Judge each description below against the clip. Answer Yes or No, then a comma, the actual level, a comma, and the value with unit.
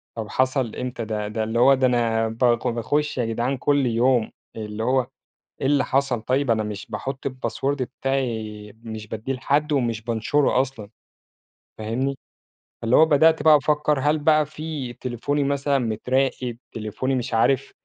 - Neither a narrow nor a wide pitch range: Yes, average, 3.5 semitones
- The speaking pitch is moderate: No, low, 130 Hz